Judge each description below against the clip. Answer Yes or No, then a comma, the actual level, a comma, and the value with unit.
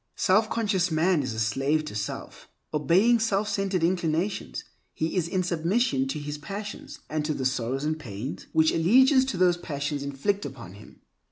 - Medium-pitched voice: Yes, medium, 160 Hz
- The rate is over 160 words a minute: Yes, average, 175 wpm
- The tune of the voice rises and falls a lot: Yes, wide, 5.7 semitones